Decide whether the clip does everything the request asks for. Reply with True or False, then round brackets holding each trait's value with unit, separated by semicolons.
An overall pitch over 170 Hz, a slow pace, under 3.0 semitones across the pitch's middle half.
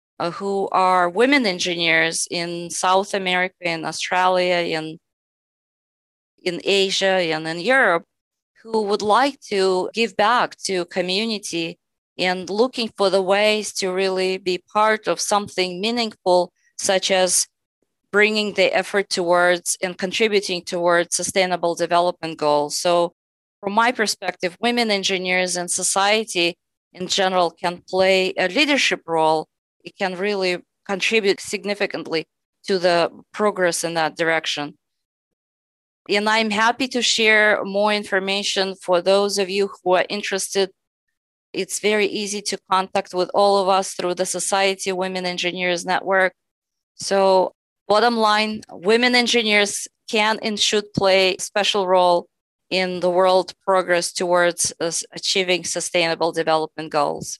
True (185 Hz; 130 wpm; 2.5 semitones)